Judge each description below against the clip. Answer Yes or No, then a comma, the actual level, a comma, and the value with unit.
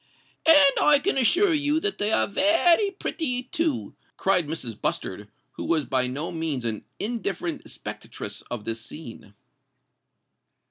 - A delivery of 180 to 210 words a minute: No, average, 140 wpm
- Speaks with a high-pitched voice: Yes, high, 210 Hz